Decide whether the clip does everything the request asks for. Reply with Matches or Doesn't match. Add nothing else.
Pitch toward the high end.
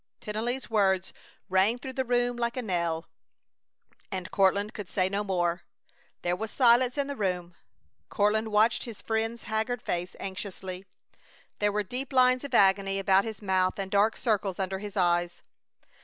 Matches